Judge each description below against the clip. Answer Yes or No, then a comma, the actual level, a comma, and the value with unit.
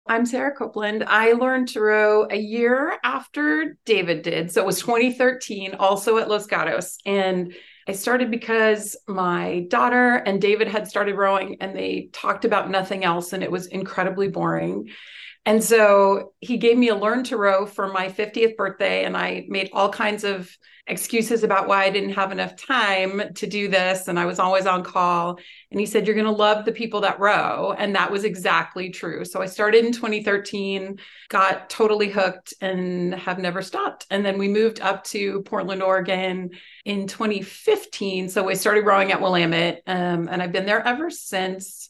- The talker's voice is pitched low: No, high, 200 Hz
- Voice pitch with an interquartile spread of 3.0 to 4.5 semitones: No, narrow, 2.5 semitones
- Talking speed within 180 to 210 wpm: Yes, average, 185 wpm